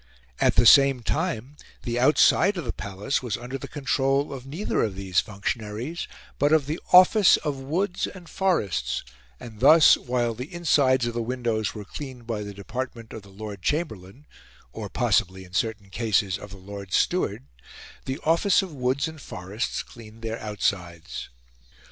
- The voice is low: Yes, low, 120 Hz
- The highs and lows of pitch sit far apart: Yes, wide, 5.8 semitones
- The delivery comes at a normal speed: Yes, average, 165 wpm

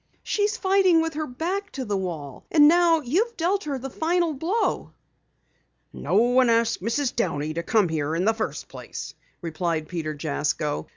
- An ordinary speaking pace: Yes, average, 170 wpm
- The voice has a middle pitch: No, very high, 250 Hz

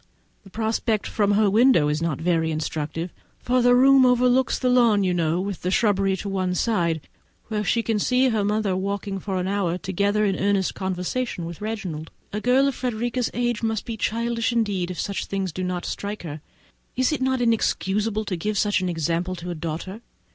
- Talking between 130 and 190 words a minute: No, average, 200 wpm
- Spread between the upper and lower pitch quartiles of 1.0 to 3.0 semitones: No, average, 4.2 semitones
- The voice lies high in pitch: Yes, high, 200 Hz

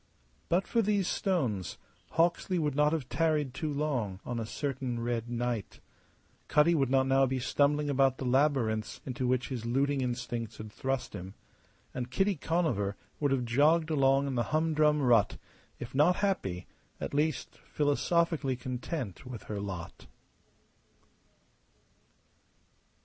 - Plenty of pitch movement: No, average, 4.0 semitones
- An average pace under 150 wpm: Yes, average, 140 wpm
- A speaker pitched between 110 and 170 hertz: Yes, low, 135 Hz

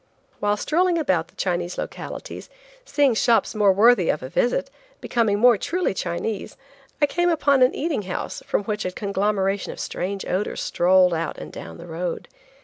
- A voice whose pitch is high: Yes, high, 205 Hz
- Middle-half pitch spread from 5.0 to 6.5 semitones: Yes, wide, 5.5 semitones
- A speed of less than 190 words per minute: Yes, average, 165 wpm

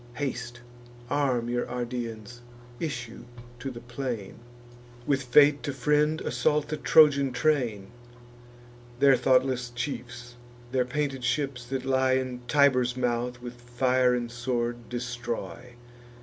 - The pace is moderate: No, slow, 120 wpm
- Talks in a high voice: No, low, 125 Hz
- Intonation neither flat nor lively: No, narrow, 2.1 semitones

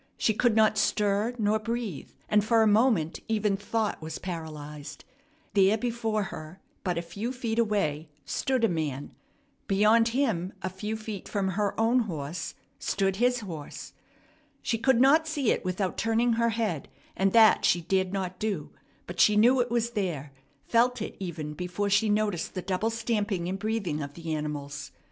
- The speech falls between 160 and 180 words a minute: Yes, average, 170 wpm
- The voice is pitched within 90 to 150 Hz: No, high, 205 Hz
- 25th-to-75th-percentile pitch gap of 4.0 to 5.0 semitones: Yes, average, 4.4 semitones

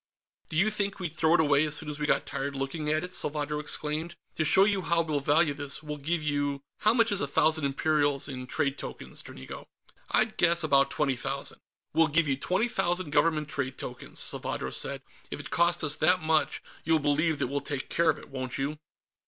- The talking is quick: Yes, fast, 215 wpm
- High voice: No, medium, 150 Hz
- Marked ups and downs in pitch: No, average, 2.8 semitones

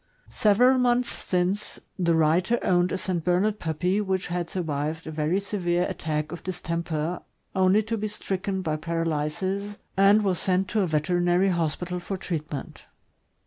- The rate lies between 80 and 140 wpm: No, average, 155 wpm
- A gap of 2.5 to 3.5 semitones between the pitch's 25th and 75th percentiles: Yes, average, 3.1 semitones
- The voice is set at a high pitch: No, medium, 180 Hz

